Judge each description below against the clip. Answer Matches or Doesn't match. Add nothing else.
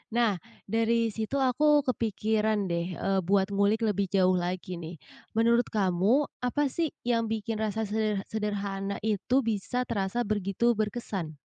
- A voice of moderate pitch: Doesn't match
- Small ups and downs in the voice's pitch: Doesn't match